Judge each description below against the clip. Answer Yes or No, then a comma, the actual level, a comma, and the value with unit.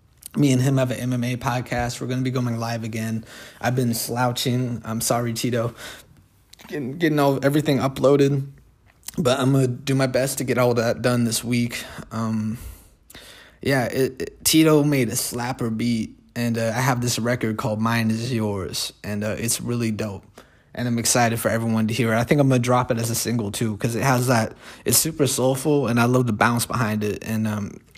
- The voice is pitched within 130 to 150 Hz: No, low, 120 Hz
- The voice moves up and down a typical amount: No, narrow, 2.3 semitones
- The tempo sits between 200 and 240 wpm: Yes, fast, 205 wpm